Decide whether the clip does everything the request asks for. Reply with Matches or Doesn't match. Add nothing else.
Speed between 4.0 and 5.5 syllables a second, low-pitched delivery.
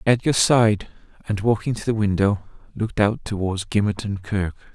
Matches